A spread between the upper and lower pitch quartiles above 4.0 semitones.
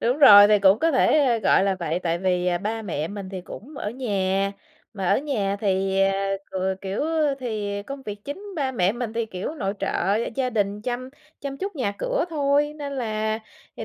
Yes: average, 5.2 semitones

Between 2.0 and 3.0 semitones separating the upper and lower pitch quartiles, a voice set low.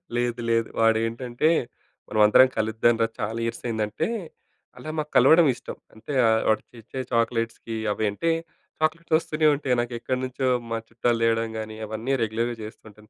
Yes: narrow, 2.6 semitones; low, 115 Hz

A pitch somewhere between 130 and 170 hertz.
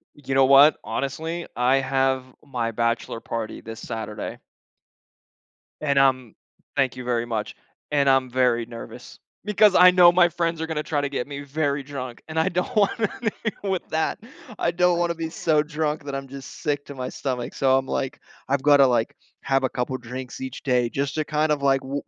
Yes: medium, 140 Hz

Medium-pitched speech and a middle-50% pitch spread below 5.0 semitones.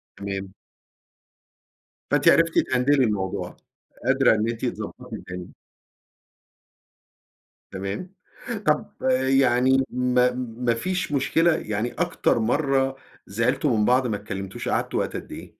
No: low, 125 Hz; average, 4.3 semitones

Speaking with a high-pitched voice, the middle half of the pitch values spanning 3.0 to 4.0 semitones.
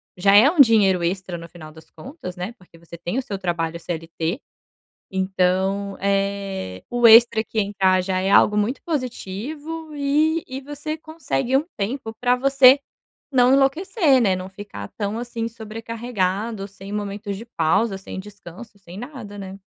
No: high, 205 Hz; average, 5.0 semitones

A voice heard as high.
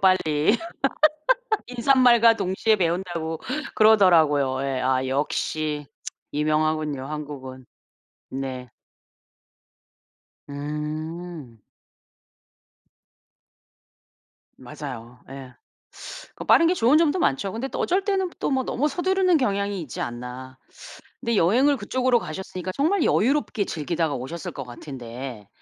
No: medium, 160 Hz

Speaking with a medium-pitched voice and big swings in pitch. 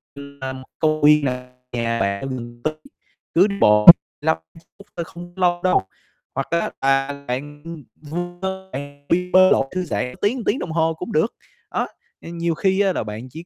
No: medium, 155 Hz; average, 4.9 semitones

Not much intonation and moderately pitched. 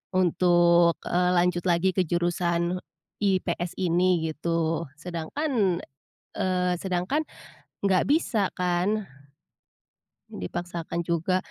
Yes: narrow, 1.5 semitones; medium, 175 Hz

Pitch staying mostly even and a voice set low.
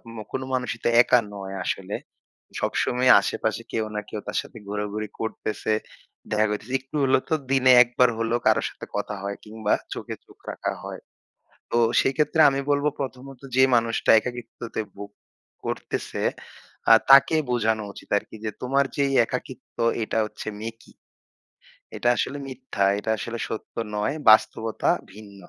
No: average, 3.3 semitones; low, 115 Hz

